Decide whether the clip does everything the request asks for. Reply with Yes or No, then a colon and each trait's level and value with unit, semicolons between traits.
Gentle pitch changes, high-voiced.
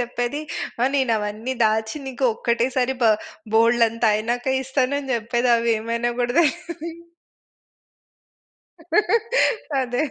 Yes: narrow, 2.2 semitones; high, 240 Hz